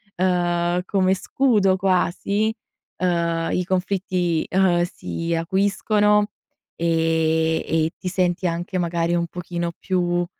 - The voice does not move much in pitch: Yes, narrow, 1.9 semitones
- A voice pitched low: No, medium, 175 Hz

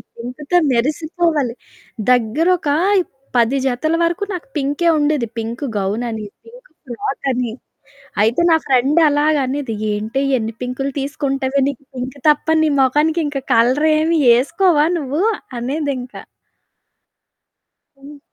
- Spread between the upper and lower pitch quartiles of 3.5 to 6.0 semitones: Yes, average, 3.9 semitones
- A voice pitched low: No, very high, 275 Hz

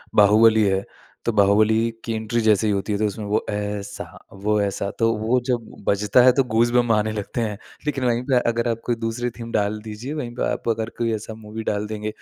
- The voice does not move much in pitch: Yes, narrow, 2.0 semitones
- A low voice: Yes, low, 110 Hz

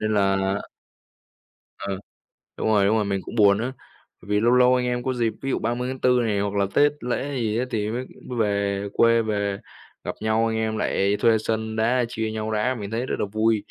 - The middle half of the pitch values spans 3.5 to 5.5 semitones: No, average, 2.8 semitones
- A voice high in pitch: No, low, 110 Hz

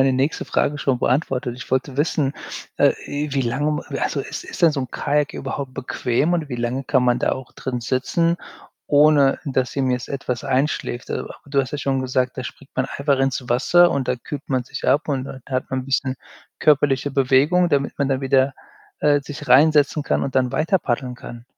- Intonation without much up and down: Yes, narrow, 2.2 semitones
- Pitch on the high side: No, low, 135 Hz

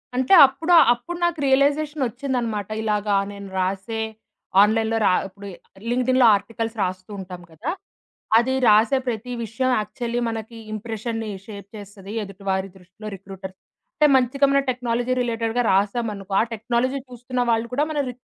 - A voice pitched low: No, high, 225 Hz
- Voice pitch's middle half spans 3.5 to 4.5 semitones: Yes, average, 3.8 semitones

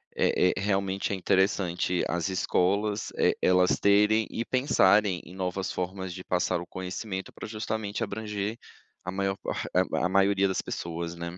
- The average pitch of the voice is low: Yes, very low, 95 Hz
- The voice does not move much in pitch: Yes, narrow, 2.0 semitones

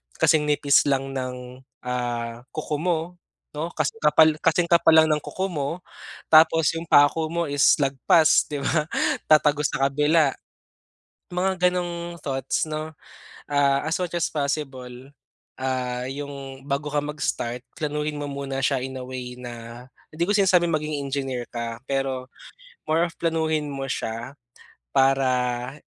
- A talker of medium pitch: Yes, medium, 145 Hz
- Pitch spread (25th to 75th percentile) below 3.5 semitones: Yes, average, 3.1 semitones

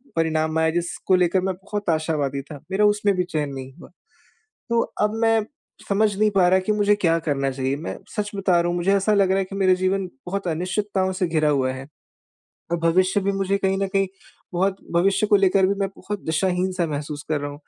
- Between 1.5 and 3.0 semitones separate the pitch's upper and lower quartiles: No, average, 3.7 semitones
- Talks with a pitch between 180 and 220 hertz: Yes, medium, 185 Hz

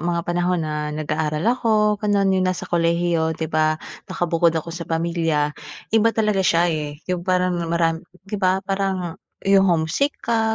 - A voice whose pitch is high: No, medium, 175 Hz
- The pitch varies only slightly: No, average, 3.1 semitones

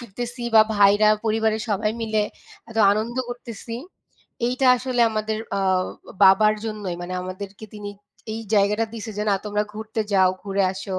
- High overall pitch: Yes, high, 215 Hz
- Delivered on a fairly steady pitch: Yes, narrow, 1.9 semitones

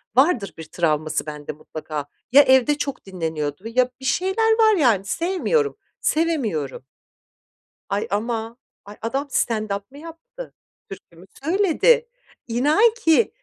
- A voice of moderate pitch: No, very high, 250 Hz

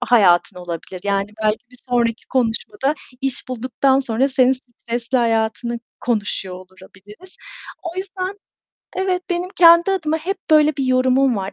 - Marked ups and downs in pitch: Yes, wide, 5.7 semitones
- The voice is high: Yes, very high, 250 Hz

